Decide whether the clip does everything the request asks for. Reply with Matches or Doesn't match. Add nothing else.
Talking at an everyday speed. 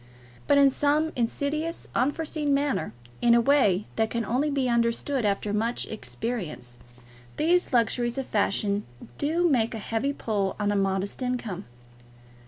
Matches